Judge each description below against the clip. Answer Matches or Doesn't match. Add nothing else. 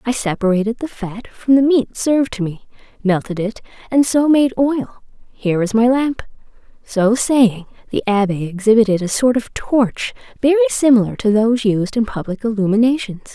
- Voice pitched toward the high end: Matches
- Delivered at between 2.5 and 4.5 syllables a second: Doesn't match